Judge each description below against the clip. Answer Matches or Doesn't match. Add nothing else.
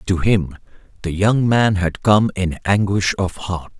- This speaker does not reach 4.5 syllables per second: Matches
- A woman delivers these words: Doesn't match